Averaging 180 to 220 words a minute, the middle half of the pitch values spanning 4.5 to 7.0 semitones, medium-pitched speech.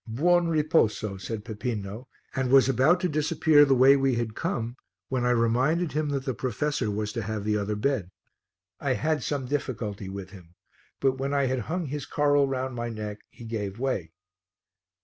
No: average, 185 wpm; average, 4.8 semitones; low, 130 Hz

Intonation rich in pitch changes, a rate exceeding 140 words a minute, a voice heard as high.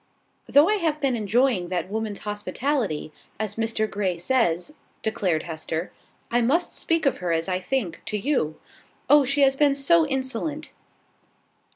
Yes: wide, 7.3 semitones; average, 155 wpm; high, 230 Hz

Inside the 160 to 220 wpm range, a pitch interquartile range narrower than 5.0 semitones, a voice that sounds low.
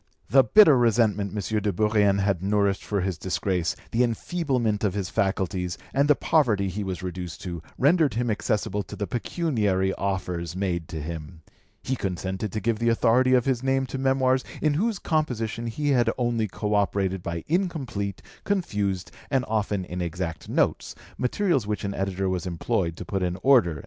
No: average, 175 wpm; average, 5.3 semitones; low, 105 Hz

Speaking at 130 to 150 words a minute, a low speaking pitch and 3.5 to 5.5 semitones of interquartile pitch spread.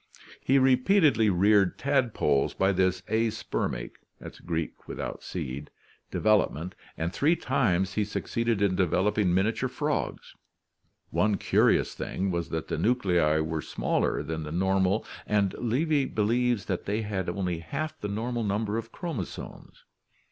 Yes: average, 145 wpm; low, 100 Hz; average, 4.8 semitones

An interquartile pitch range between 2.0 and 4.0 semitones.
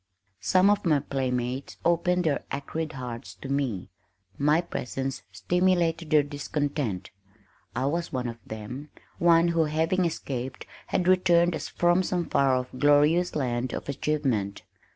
No: average, 4.8 semitones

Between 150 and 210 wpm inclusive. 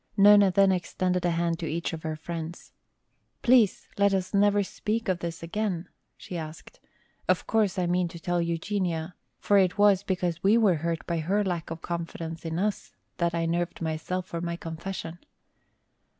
Yes: average, 180 wpm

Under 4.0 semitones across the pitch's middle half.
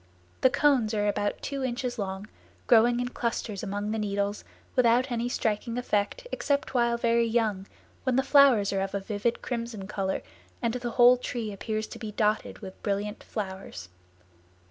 Yes: average, 3.1 semitones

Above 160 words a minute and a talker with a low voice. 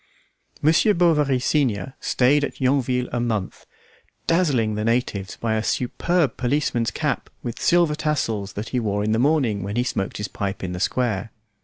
Yes: average, 170 wpm; low, 120 Hz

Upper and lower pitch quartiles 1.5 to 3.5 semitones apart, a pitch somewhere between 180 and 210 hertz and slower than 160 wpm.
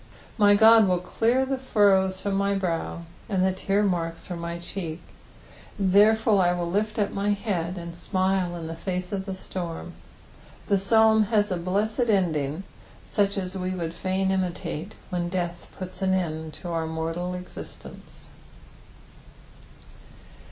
Yes: average, 2.8 semitones; medium, 185 Hz; average, 150 wpm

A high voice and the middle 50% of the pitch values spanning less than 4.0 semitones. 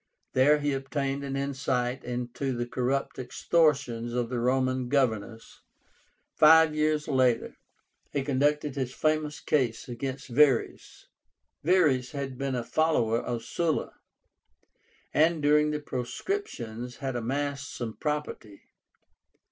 No: low, 135 Hz; average, 3.3 semitones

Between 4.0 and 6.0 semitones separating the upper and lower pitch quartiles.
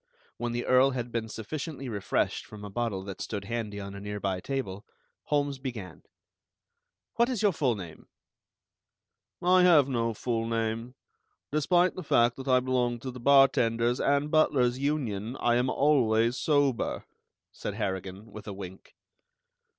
Yes: average, 4.3 semitones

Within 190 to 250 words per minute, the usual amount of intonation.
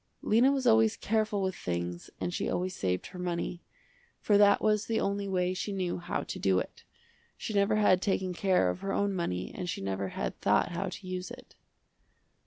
Yes: average, 200 wpm; average, 3.0 semitones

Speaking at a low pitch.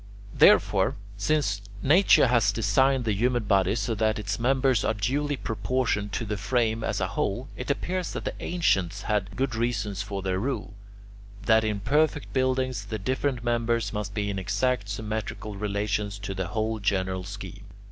Yes: low, 110 Hz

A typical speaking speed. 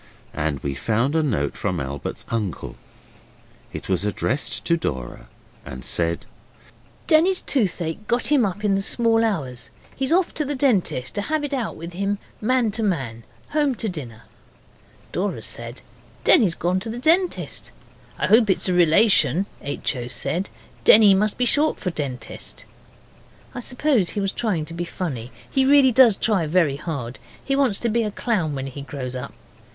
Yes: average, 175 wpm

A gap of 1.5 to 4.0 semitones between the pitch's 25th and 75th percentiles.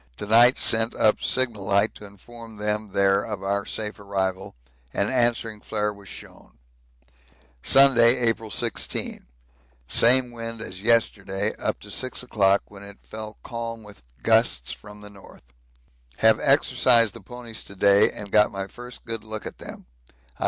Yes: narrow, 2.5 semitones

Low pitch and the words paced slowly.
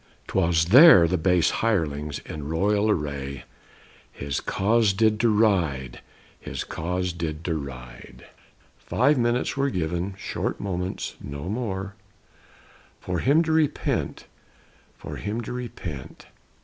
Yes: very low, 90 Hz; slow, 115 wpm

